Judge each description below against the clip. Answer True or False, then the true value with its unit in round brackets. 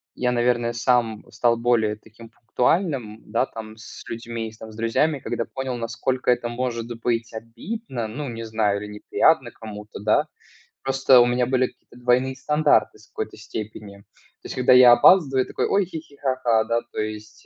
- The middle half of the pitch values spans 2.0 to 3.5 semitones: True (2.5 semitones)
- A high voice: False (120 Hz)